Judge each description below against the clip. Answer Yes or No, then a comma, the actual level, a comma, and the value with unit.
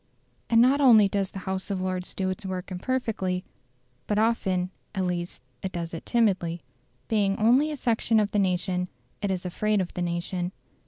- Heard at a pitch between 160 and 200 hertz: Yes, high, 190 Hz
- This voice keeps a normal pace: Yes, average, 180 wpm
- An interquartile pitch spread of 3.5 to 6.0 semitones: No, average, 3.1 semitones